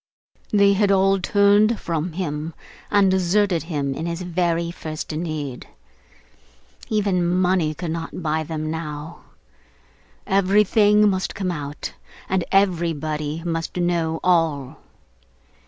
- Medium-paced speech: No, slow, 115 wpm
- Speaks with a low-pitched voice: No, medium, 170 Hz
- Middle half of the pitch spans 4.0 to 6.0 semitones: No, average, 3.4 semitones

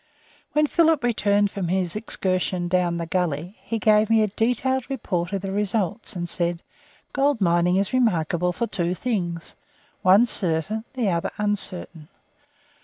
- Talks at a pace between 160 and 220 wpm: No, average, 150 wpm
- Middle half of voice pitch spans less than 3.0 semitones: No, average, 4.2 semitones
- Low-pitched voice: No, high, 195 Hz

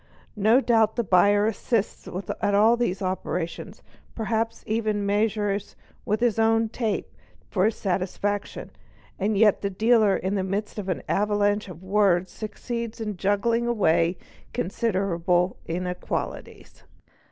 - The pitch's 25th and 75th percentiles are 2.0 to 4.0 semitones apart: Yes, average, 2.7 semitones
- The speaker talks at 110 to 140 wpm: Yes, slow, 135 wpm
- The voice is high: Yes, high, 205 Hz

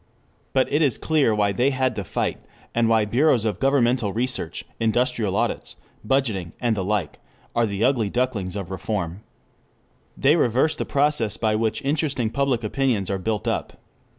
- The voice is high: No, low, 115 Hz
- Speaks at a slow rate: No, average, 165 wpm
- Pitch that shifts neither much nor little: Yes, average, 4.2 semitones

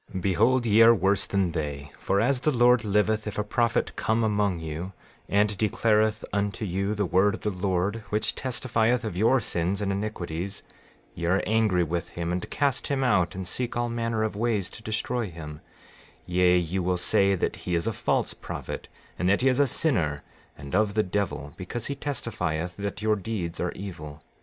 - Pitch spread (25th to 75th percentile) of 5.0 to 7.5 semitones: No, average, 4.0 semitones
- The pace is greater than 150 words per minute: Yes, average, 195 wpm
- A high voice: No, low, 100 Hz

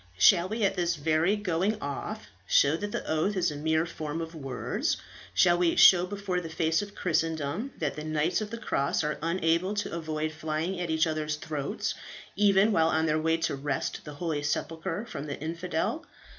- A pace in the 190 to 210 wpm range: Yes, average, 195 wpm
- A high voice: No, medium, 165 Hz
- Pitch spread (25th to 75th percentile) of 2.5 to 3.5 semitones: Yes, average, 3.1 semitones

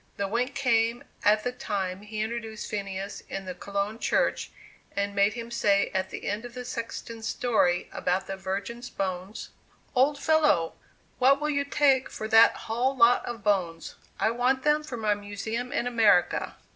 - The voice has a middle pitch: No, high, 225 Hz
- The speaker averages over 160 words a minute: Yes, average, 170 wpm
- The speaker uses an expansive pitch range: No, average, 3.7 semitones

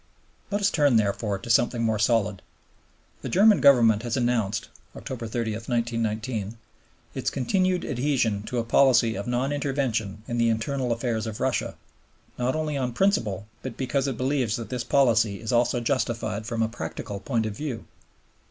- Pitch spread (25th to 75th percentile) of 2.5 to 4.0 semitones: Yes, average, 3.2 semitones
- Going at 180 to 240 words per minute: No, average, 165 wpm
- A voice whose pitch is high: No, low, 120 Hz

